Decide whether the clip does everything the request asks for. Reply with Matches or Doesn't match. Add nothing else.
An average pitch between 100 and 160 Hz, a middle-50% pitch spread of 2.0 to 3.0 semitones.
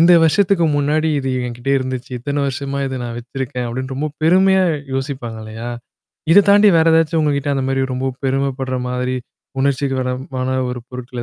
Matches